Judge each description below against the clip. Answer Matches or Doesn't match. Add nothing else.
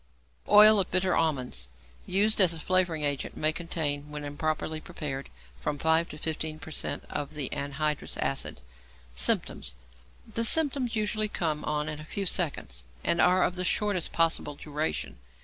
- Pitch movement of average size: Matches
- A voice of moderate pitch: Matches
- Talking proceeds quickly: Doesn't match